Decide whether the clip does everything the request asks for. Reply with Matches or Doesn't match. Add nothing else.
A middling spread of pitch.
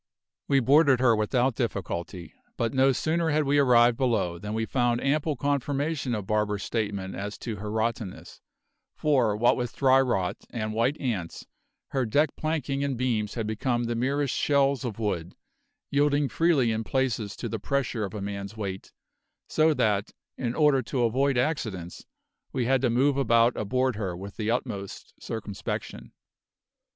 Matches